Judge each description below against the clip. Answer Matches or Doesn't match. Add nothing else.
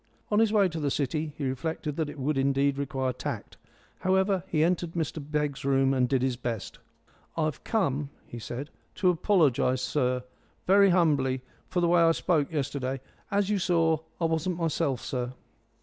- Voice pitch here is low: Doesn't match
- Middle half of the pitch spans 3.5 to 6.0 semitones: Matches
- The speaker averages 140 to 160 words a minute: Doesn't match